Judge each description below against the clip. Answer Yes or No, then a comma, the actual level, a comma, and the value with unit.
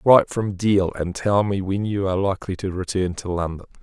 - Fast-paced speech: Yes, fast, 220 wpm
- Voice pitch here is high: No, very low, 95 Hz